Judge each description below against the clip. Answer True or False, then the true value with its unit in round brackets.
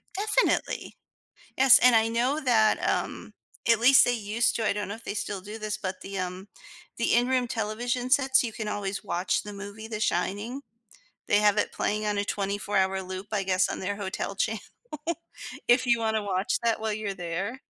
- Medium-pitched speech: False (215 Hz)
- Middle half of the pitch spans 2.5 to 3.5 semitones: True (3.0 semitones)